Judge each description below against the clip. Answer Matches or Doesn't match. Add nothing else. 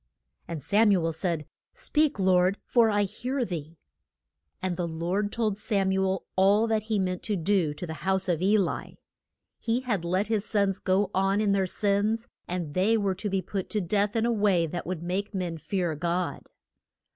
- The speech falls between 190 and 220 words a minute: Matches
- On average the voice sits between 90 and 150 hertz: Doesn't match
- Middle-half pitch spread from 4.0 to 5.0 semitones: Doesn't match